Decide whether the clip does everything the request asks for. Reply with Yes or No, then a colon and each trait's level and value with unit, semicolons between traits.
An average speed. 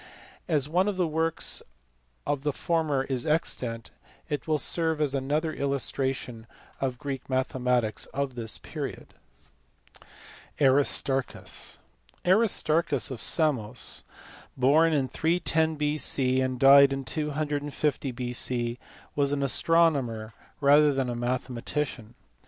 No: slow, 115 wpm